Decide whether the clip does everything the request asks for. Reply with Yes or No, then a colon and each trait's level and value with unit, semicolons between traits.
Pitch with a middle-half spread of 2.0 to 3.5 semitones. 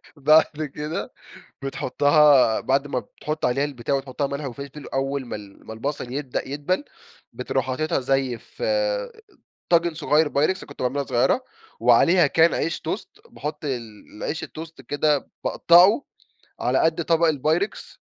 Yes: average, 3.0 semitones